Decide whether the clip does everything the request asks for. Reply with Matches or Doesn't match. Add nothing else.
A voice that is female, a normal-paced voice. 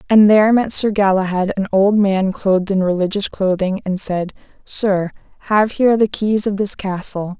Matches